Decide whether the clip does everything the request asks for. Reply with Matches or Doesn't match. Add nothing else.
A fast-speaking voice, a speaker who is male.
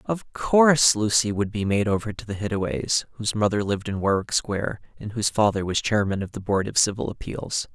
Matches